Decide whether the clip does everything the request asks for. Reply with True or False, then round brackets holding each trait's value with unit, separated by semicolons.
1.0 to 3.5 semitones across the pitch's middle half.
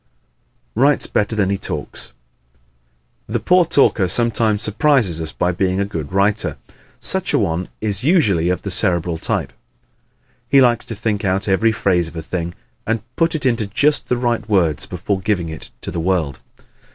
False (4.8 semitones)